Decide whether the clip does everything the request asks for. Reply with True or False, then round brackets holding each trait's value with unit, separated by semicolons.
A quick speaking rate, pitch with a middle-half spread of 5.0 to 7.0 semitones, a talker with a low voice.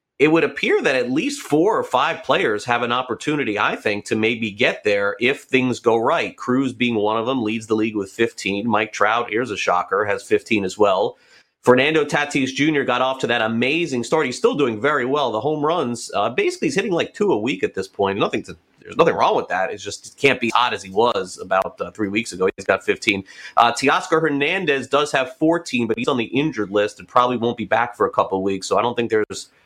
True (245 wpm; 5.4 semitones; 125 Hz)